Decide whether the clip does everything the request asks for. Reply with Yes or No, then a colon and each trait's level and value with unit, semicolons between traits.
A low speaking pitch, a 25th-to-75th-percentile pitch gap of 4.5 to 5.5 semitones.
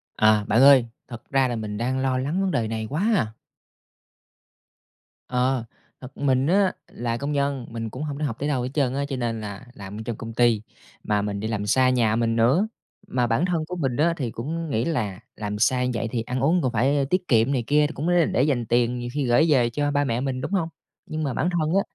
No: low, 130 Hz; average, 4.0 semitones